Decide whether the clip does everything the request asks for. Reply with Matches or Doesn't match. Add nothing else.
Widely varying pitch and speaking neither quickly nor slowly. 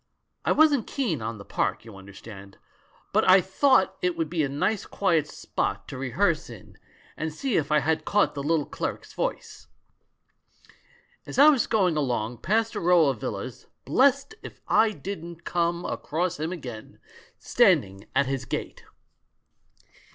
Matches